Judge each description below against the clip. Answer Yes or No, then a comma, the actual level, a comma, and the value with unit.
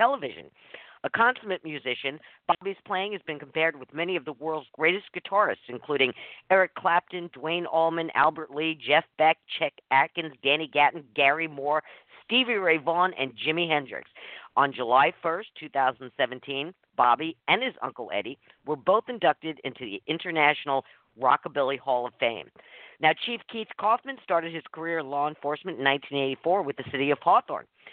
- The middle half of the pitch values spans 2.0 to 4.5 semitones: Yes, average, 3.8 semitones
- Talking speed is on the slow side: No, average, 165 wpm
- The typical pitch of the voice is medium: Yes, medium, 155 Hz